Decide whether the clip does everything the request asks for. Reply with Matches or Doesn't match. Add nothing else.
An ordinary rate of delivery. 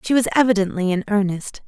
Matches